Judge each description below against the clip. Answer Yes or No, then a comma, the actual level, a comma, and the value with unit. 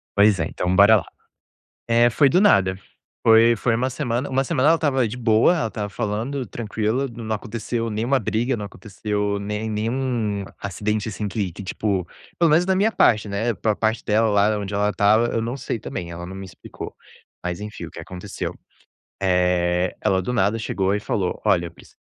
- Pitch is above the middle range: No, low, 110 Hz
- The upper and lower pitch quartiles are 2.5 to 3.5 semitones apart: Yes, average, 3.0 semitones